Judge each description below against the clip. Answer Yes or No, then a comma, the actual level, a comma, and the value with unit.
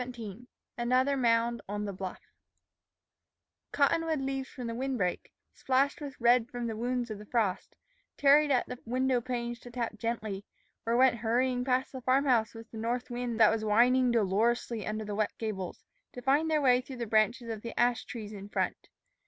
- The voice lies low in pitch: No, high, 240 Hz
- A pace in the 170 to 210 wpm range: Yes, average, 190 wpm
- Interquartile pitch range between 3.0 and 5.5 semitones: No, narrow, 2.6 semitones